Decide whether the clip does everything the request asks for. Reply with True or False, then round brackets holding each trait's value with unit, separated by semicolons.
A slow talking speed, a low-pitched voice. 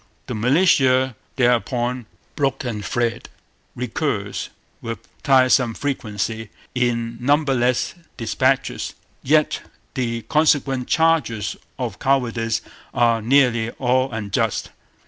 True (90 wpm; 125 Hz)